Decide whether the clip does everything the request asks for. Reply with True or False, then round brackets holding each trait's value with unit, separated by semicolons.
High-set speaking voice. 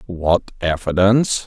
False (95 Hz)